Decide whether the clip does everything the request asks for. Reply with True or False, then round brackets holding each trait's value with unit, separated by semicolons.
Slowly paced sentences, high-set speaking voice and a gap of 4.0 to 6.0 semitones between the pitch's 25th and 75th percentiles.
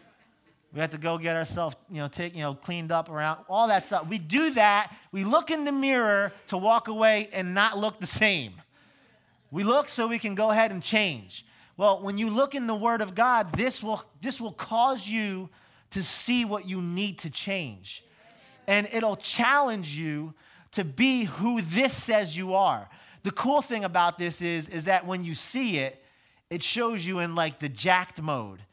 False (200 wpm; 195 Hz; 5.3 semitones)